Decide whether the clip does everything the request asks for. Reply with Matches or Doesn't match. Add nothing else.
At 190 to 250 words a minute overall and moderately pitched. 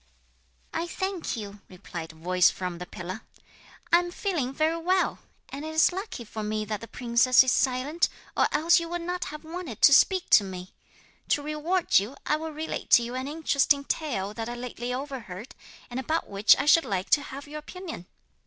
Doesn't match